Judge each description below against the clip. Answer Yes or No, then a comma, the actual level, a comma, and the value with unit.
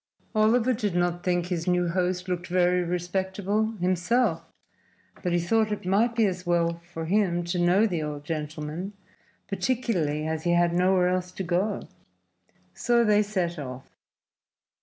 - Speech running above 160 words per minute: No, average, 155 wpm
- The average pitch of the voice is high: No, medium, 180 Hz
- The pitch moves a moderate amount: Yes, average, 3.0 semitones